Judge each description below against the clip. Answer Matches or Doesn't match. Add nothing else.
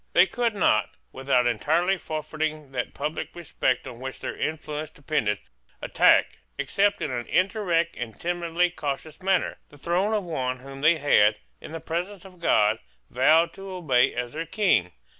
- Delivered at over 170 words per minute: Doesn't match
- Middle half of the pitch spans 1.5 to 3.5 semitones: Doesn't match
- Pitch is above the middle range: Doesn't match